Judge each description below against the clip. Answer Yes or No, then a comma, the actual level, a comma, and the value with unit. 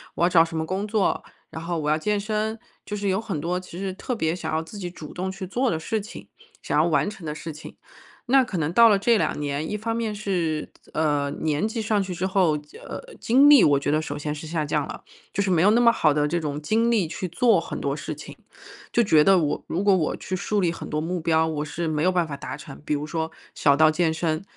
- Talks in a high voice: No, medium, 175 Hz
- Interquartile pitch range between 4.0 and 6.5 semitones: Yes, average, 4.9 semitones